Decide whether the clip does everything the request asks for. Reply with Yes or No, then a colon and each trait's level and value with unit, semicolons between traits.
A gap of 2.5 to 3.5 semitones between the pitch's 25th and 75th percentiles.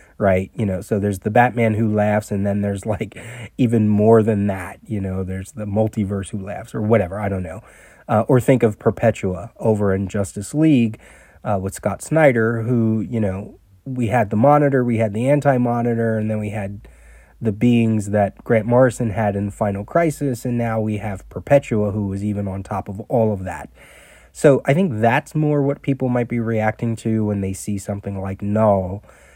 Yes: average, 2.9 semitones